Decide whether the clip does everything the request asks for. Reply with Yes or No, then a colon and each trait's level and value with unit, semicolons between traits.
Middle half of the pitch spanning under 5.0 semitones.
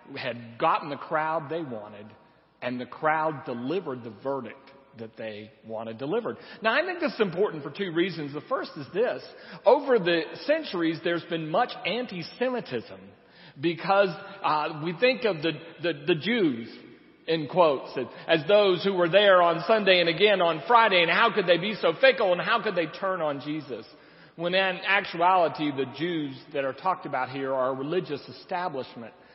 No: wide, 5.6 semitones